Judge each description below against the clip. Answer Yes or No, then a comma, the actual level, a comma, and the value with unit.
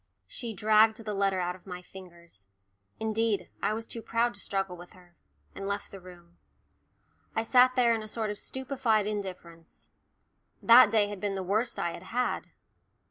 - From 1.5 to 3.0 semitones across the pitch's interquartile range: No, average, 3.6 semitones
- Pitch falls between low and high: No, high, 205 Hz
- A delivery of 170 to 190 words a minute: Yes, average, 180 wpm